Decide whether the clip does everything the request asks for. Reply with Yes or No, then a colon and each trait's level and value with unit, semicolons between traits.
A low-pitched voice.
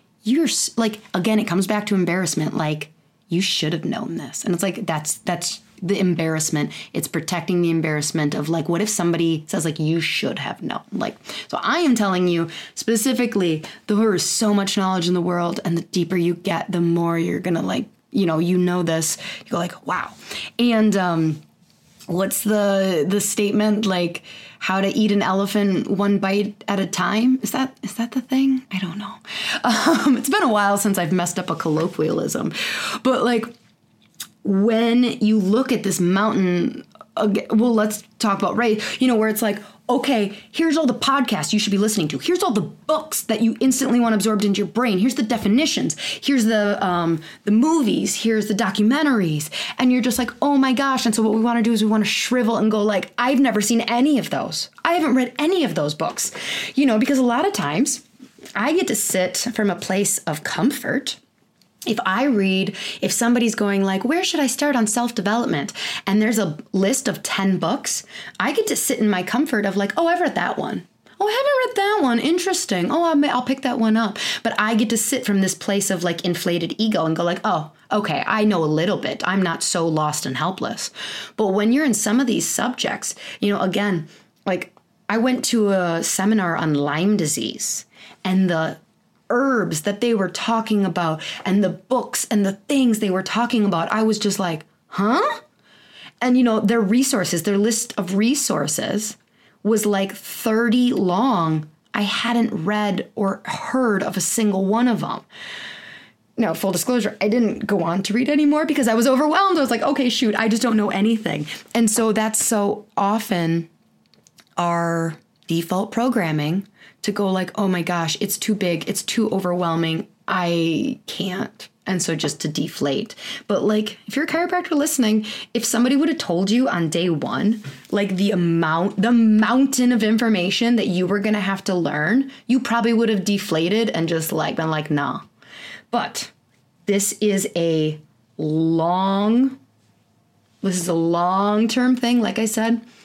No: high, 210 Hz